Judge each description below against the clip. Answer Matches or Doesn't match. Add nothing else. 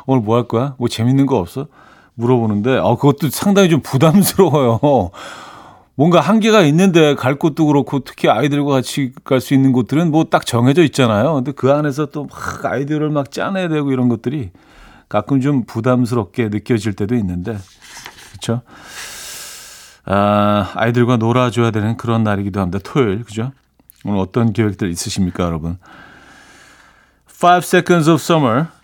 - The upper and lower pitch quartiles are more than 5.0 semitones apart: Doesn't match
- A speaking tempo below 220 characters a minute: Doesn't match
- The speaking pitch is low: Matches